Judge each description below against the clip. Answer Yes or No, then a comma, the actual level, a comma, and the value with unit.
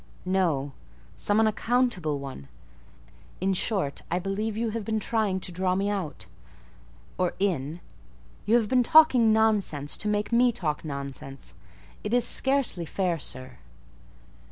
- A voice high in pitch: Yes, high, 195 Hz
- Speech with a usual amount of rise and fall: No, wide, 6.6 semitones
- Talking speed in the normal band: No, slow, 130 wpm